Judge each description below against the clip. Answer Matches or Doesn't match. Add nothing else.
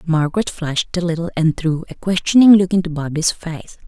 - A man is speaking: Doesn't match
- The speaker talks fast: Doesn't match